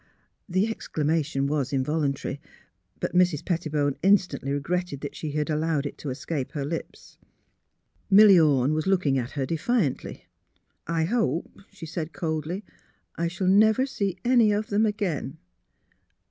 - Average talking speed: Yes, average, 155 wpm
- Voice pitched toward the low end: No, medium, 160 Hz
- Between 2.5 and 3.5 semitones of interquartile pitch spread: No, average, 4.9 semitones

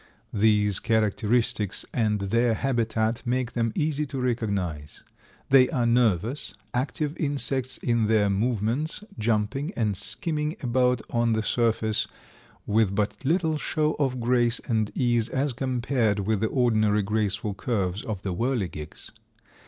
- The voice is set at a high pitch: No, low, 115 Hz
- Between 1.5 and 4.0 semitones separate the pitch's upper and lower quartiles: Yes, average, 3.3 semitones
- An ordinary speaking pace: No, slow, 130 wpm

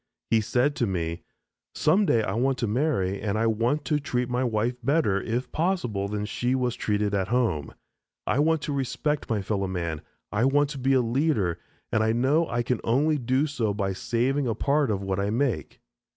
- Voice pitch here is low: Yes, low, 120 Hz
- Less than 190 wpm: No, fast, 205 wpm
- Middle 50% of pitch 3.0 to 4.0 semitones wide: No, average, 5.0 semitones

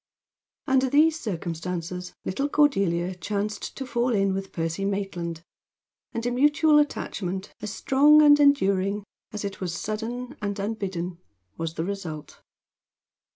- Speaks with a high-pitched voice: Yes, high, 200 Hz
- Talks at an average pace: No, slow, 130 wpm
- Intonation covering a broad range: Yes, wide, 5.9 semitones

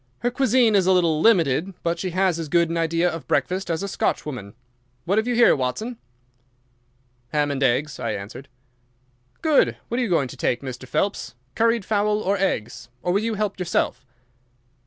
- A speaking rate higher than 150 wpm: Yes, average, 185 wpm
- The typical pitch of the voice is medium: Yes, medium, 175 Hz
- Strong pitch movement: Yes, wide, 6.7 semitones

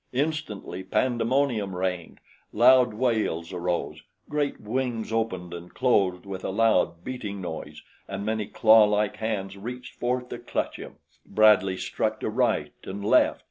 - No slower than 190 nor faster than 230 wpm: No, average, 140 wpm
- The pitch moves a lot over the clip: No, average, 4.5 semitones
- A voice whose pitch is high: No, low, 110 Hz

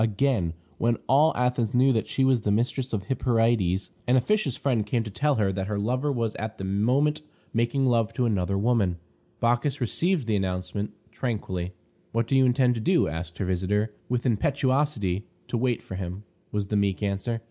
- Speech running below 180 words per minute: No, average, 190 wpm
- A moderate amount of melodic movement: Yes, average, 4.2 semitones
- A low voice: Yes, low, 115 Hz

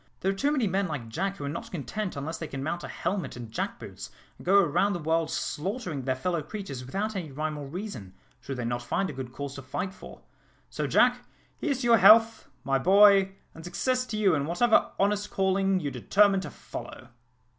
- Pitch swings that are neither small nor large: No, wide, 6.1 semitones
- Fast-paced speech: Yes, fast, 210 wpm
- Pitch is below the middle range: No, medium, 180 Hz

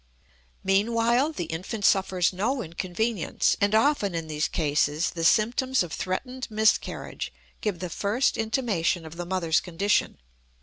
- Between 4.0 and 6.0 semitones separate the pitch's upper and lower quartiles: Yes, average, 5.1 semitones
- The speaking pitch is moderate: No, high, 195 Hz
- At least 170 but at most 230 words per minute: No, slow, 135 wpm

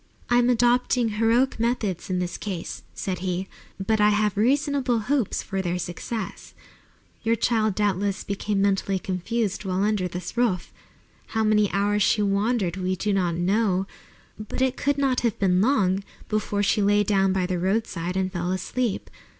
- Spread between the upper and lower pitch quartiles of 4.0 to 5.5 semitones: No, average, 3.4 semitones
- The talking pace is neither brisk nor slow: Yes, average, 165 wpm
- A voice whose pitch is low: No, high, 205 Hz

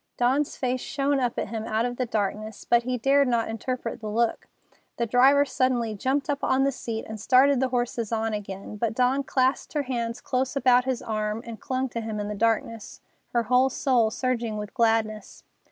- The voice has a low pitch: No, high, 240 Hz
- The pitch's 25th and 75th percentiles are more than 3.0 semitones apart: No, average, 2.7 semitones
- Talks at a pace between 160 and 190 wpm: No, average, 200 wpm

